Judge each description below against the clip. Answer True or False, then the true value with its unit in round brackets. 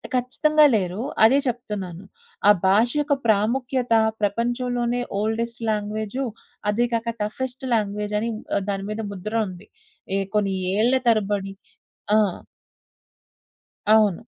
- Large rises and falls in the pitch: False (2.9 semitones)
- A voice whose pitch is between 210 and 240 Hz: True (220 Hz)